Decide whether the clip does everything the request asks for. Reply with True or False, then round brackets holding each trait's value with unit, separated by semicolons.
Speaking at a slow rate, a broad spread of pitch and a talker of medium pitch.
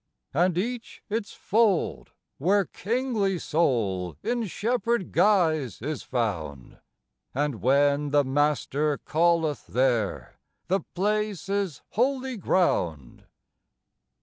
True (95 wpm; 7.6 semitones; 165 Hz)